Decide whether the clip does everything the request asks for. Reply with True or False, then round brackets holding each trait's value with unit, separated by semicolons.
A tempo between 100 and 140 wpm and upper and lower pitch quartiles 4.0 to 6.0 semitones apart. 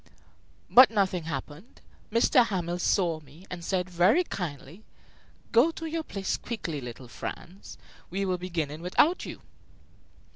True (135 wpm; 4.9 semitones)